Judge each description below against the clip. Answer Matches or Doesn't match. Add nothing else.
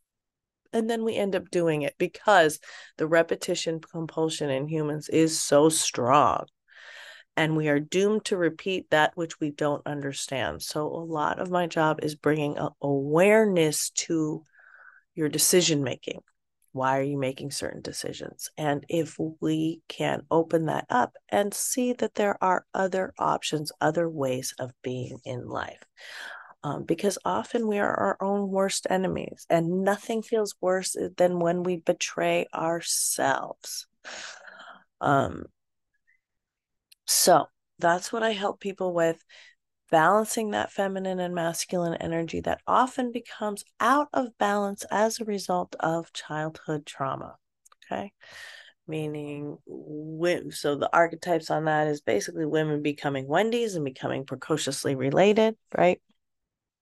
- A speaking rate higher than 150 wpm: Doesn't match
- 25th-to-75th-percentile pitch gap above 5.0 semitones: Doesn't match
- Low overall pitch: Doesn't match